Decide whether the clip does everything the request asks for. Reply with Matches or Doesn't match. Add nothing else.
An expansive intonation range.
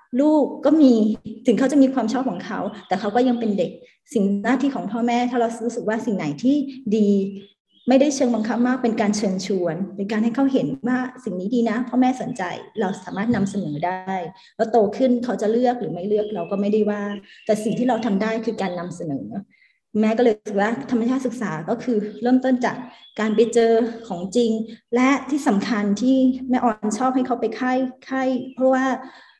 Doesn't match